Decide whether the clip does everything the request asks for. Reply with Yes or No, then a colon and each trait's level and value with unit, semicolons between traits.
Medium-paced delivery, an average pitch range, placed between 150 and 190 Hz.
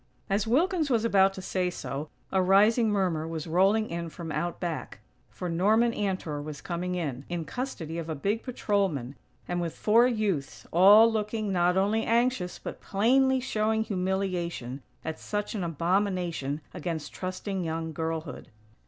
Yes: average, 155 wpm; average, 4.5 semitones; medium, 185 Hz